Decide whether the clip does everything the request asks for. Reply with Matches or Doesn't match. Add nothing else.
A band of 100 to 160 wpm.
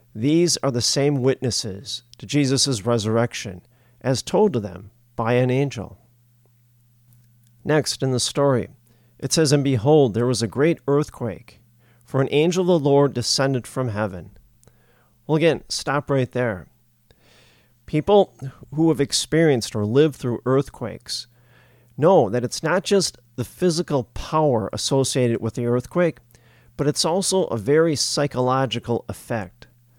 Matches